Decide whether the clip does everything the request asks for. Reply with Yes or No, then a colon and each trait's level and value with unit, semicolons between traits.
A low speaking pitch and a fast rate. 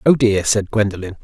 No: low, 105 Hz; average, 195 wpm